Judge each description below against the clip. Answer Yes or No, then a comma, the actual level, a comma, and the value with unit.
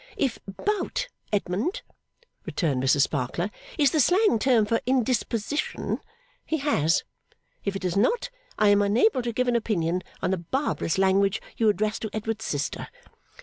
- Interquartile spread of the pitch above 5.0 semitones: Yes, wide, 5.5 semitones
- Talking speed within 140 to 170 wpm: Yes, average, 150 wpm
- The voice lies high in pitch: Yes, high, 215 Hz